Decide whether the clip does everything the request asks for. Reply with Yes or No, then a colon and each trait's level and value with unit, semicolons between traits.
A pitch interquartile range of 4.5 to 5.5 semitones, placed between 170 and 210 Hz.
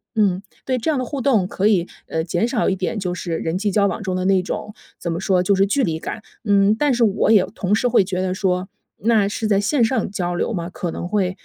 No: average, 3.2 semitones; high, 195 Hz